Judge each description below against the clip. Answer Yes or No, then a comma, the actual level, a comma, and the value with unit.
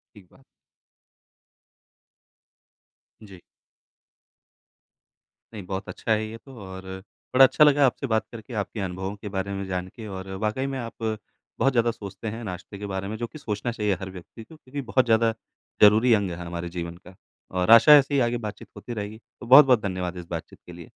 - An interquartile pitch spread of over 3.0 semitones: Yes, average, 3.9 semitones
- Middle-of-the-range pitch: No, low, 105 Hz